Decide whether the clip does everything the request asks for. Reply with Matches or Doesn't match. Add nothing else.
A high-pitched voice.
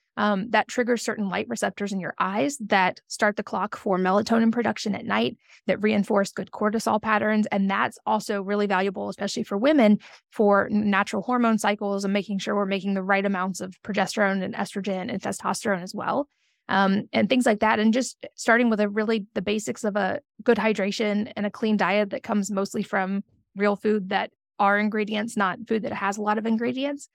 Matches